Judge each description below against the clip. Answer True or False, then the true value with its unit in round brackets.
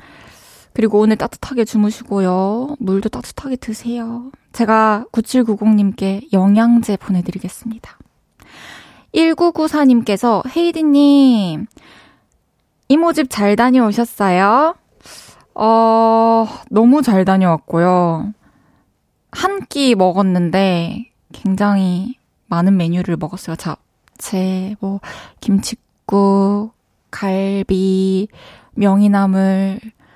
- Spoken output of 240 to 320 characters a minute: False (185 characters per minute)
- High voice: True (210 Hz)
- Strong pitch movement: False (3.6 semitones)